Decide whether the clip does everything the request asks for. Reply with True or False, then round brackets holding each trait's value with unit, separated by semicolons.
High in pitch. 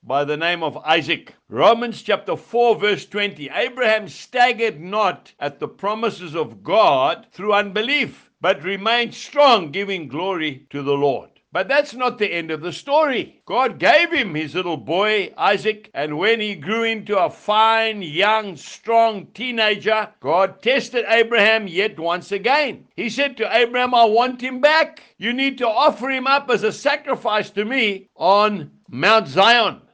True (215 Hz)